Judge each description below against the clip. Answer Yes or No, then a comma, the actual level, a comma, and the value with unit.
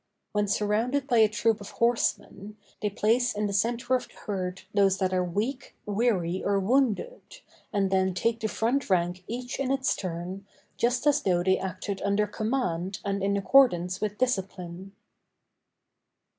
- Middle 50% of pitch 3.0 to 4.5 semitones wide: Yes, average, 3.9 semitones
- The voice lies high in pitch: Yes, high, 205 Hz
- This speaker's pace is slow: No, average, 160 wpm